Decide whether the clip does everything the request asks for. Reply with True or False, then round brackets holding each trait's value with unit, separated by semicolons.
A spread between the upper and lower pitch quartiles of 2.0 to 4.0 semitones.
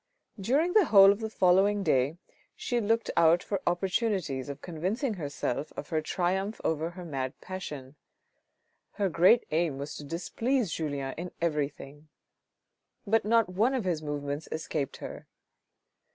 False (5.5 semitones)